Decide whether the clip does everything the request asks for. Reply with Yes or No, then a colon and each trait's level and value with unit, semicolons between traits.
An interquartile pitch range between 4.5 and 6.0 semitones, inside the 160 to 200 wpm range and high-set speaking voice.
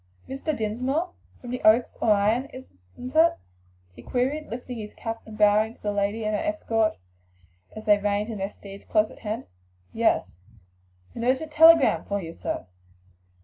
No: average, 3.8 semitones; average, 165 wpm; high, 225 Hz